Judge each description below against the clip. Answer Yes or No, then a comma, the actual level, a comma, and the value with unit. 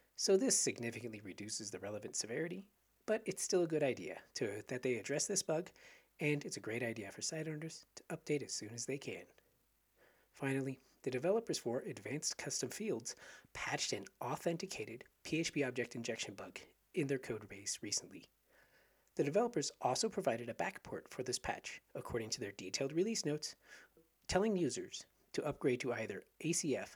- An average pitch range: No, wide, 6.4 semitones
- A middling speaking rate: Yes, average, 165 wpm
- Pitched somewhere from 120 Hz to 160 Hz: Yes, medium, 140 Hz